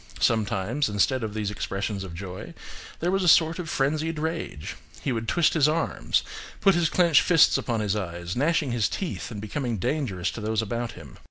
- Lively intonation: Yes, wide, 7.4 semitones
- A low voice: Yes, low, 120 Hz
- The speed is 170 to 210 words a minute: Yes, average, 190 wpm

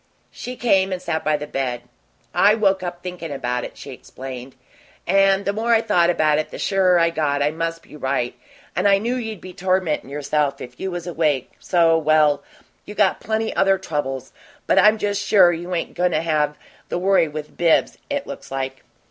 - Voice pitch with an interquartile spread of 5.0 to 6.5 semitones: No, average, 4.6 semitones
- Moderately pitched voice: Yes, medium, 170 Hz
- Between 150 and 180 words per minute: No, average, 200 wpm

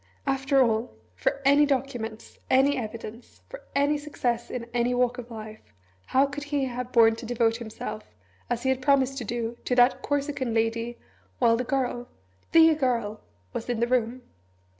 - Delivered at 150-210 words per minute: Yes, average, 170 wpm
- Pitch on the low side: No, high, 245 Hz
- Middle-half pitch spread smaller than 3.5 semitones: Yes, average, 2.9 semitones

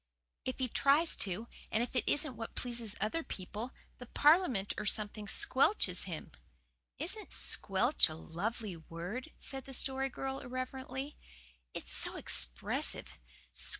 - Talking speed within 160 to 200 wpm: No, slow, 135 wpm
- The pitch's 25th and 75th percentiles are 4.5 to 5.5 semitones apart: Yes, average, 5.2 semitones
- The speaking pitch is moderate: No, high, 240 Hz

